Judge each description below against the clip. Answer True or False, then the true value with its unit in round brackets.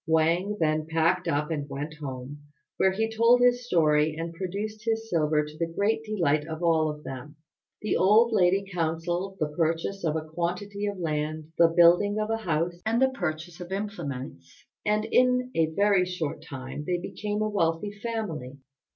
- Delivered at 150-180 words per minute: True (175 wpm)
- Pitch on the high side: False (170 Hz)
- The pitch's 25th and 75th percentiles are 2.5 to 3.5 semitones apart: False (4.9 semitones)